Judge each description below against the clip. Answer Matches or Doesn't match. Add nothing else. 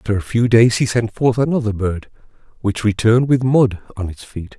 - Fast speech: Matches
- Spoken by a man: Matches